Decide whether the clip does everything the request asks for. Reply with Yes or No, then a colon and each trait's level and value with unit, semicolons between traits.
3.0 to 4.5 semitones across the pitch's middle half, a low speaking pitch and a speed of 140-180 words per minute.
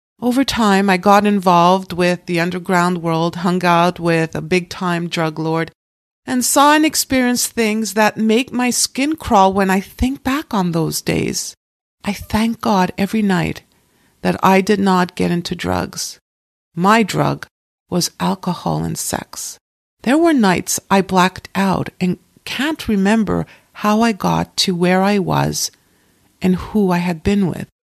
No: average, 3.8 semitones; high, 190 Hz; average, 160 wpm